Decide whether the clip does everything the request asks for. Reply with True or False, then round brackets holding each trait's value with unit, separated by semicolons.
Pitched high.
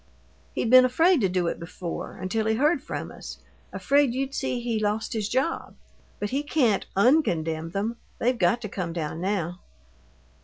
True (220 Hz)